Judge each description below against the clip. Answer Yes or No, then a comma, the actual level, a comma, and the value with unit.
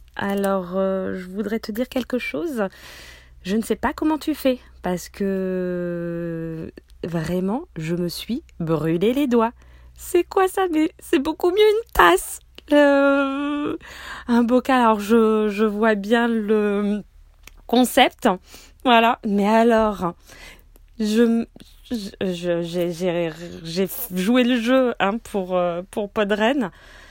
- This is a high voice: Yes, high, 220 Hz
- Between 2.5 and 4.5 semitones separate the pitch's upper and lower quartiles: No, wide, 5.5 semitones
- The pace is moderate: No, slow, 130 wpm